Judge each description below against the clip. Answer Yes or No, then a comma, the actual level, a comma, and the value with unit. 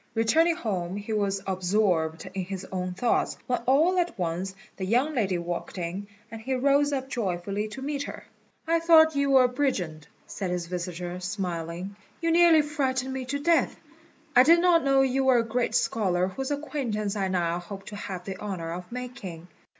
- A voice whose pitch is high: Yes, high, 210 Hz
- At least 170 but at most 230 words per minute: Yes, average, 190 wpm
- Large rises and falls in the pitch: Yes, wide, 6.8 semitones